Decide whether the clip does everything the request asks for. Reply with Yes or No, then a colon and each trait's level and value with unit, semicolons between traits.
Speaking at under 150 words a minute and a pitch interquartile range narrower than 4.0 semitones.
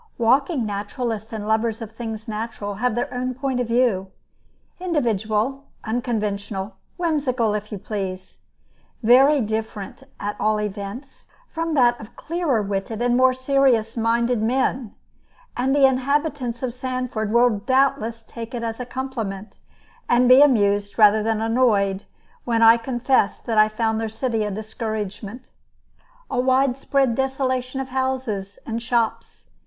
Yes: average, 140 wpm; average, 3.2 semitones